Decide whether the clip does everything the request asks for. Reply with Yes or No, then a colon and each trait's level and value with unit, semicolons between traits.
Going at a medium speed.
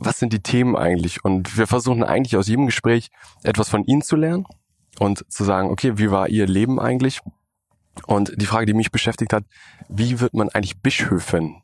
No: fast, 195 wpm